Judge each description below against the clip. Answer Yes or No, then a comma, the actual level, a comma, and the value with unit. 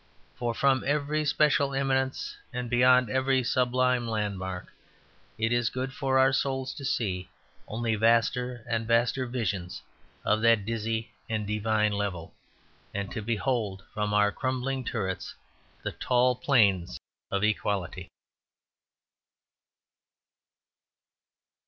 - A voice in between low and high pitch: No, low, 115 Hz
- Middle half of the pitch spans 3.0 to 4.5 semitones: Yes, average, 3.6 semitones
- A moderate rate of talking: No, slow, 115 wpm